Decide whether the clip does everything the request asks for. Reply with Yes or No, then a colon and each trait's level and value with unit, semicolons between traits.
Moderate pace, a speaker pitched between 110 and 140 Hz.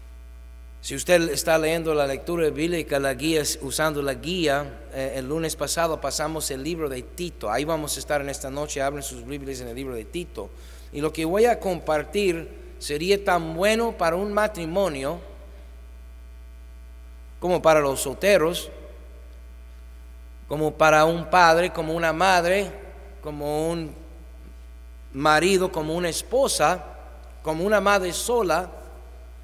No: average, 140 wpm; medium, 150 Hz